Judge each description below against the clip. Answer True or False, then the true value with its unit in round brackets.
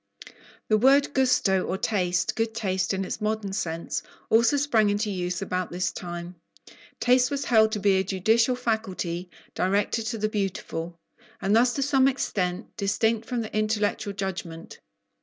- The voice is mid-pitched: False (210 Hz)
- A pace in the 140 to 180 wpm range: True (160 wpm)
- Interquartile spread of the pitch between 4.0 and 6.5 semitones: False (3.6 semitones)